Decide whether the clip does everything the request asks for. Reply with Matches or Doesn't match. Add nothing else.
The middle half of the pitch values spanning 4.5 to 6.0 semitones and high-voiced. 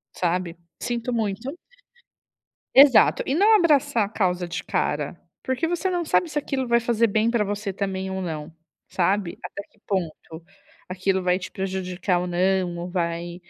Matches